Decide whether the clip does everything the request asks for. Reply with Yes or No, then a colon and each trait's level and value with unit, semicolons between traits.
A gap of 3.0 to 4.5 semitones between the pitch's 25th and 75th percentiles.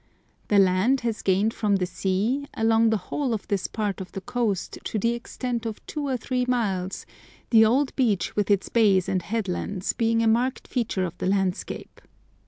Yes: average, 3.6 semitones